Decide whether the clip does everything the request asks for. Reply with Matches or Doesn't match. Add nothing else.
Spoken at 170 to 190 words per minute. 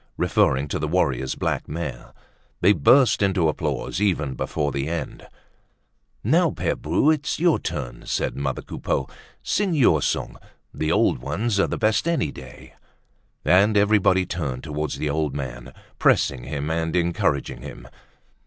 Doesn't match